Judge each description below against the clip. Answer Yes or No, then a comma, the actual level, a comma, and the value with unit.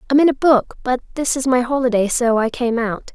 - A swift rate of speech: Yes, fast, 250 wpm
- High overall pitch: Yes, very high, 250 Hz